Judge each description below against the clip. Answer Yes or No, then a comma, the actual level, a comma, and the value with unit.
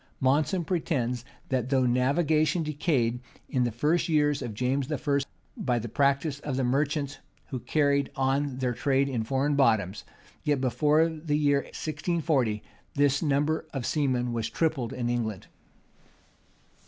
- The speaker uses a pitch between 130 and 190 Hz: Yes, medium, 140 Hz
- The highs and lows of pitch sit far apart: No, average, 3.1 semitones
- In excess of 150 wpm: No, average, 140 wpm